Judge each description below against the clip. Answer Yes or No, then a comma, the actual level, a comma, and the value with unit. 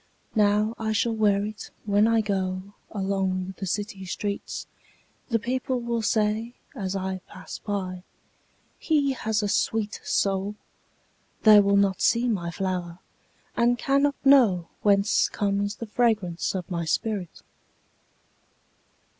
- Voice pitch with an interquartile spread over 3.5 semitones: No, average, 2.8 semitones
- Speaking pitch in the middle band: No, high, 205 Hz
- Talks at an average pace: No, slow, 105 wpm